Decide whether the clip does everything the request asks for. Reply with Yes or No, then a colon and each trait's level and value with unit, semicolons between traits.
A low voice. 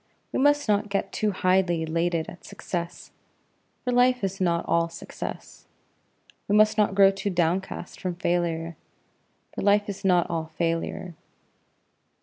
No: medium, 185 Hz